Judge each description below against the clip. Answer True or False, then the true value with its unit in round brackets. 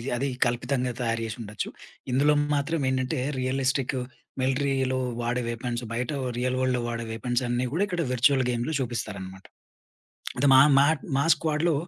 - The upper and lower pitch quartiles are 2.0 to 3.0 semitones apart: True (2.5 semitones)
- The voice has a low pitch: True (130 Hz)